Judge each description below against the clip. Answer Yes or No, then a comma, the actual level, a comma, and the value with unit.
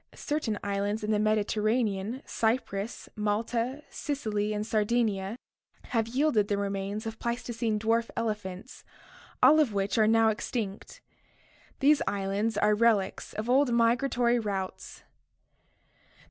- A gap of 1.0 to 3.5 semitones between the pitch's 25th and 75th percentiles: Yes, narrow, 2.5 semitones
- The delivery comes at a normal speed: No, slow, 120 wpm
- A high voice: Yes, high, 220 Hz